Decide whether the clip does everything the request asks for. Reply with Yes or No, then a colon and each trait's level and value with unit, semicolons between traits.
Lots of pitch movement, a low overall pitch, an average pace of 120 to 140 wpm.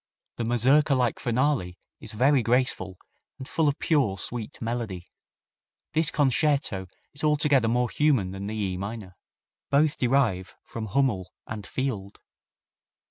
Yes: wide, 5.7 semitones; low, 120 Hz; slow, 135 wpm